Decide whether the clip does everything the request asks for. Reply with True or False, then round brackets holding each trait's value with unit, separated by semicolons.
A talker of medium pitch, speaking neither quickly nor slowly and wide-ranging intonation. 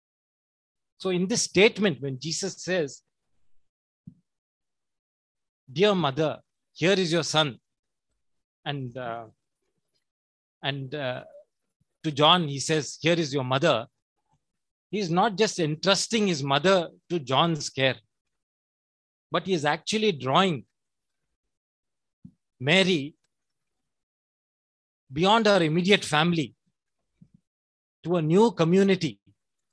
False (160 Hz; 100 wpm; 5.7 semitones)